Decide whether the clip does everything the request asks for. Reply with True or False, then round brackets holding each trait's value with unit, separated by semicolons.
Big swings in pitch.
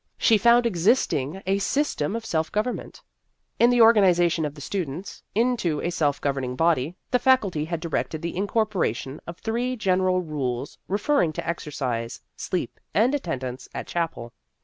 True (6.7 semitones)